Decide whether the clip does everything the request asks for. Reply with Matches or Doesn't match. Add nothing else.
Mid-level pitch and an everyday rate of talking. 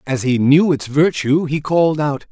Doesn't match